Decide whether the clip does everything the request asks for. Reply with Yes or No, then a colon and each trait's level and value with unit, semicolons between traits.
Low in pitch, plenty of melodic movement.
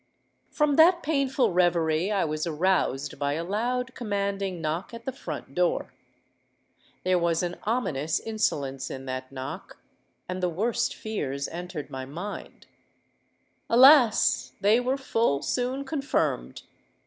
No: high, 190 Hz; wide, 7.8 semitones